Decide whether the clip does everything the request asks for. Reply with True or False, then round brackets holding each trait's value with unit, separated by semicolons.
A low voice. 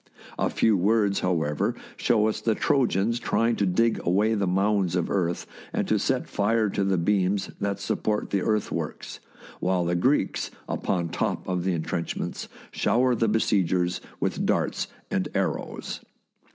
True (100 Hz)